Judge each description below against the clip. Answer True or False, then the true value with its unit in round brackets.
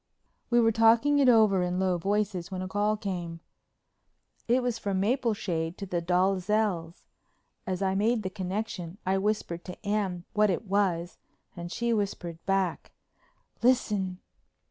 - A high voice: True (195 Hz)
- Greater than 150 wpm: False (145 wpm)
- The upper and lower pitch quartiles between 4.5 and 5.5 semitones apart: False (3.1 semitones)